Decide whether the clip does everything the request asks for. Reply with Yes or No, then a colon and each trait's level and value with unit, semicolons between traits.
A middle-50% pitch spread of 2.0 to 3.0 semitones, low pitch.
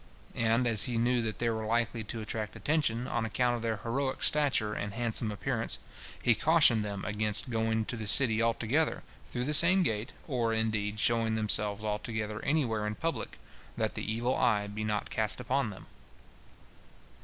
Yes: narrow, 2.4 semitones; low, 115 Hz